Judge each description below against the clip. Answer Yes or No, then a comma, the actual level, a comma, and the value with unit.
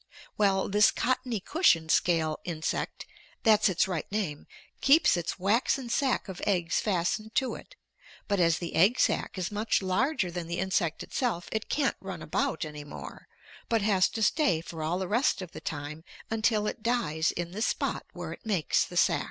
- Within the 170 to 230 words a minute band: Yes, average, 185 wpm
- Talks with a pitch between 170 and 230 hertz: Yes, high, 190 Hz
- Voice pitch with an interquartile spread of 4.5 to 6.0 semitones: Yes, average, 4.8 semitones